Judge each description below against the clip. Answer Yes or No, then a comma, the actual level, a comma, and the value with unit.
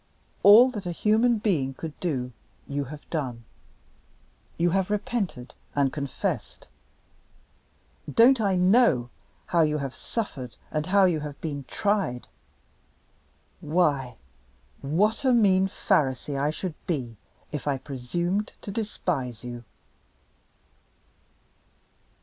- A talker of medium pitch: Yes, medium, 160 Hz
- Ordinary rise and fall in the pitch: No, wide, 6.7 semitones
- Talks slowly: Yes, slow, 115 wpm